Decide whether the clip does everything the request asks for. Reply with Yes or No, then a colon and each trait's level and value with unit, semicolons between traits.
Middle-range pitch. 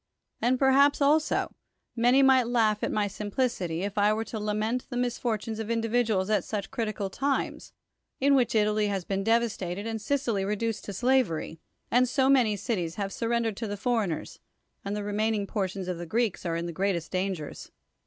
No: high, 215 Hz